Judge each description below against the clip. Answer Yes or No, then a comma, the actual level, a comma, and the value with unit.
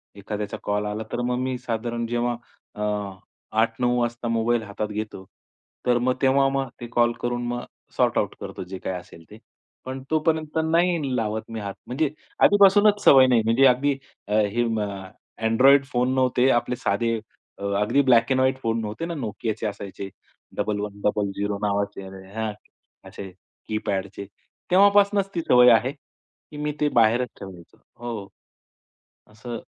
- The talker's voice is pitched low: Yes, low, 120 Hz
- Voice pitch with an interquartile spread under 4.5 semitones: Yes, average, 4.0 semitones